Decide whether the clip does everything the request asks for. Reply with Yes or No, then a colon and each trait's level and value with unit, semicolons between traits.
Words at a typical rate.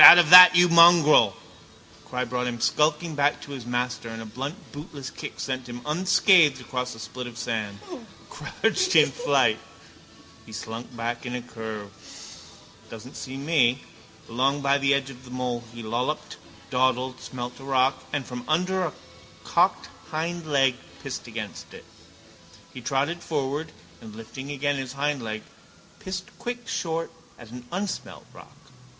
Yes: average, 155 wpm